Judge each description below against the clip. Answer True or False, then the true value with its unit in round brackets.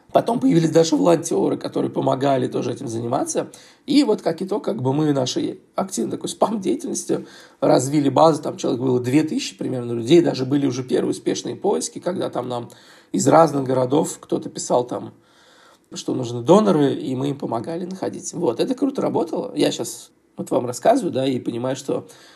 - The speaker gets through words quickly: True (175 wpm)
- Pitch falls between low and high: True (155 Hz)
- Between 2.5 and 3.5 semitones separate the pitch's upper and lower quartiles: False (5.2 semitones)